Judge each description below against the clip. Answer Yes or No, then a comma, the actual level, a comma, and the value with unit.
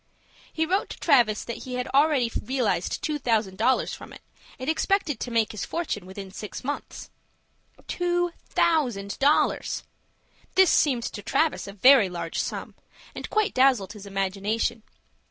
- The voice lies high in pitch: Yes, high, 245 Hz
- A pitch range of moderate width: No, wide, 6.5 semitones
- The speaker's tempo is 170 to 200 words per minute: No, average, 155 wpm